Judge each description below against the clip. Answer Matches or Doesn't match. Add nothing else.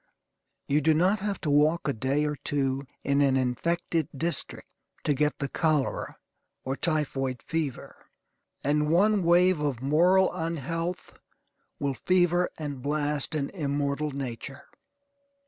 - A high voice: Doesn't match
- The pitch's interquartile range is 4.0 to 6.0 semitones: Doesn't match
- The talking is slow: Matches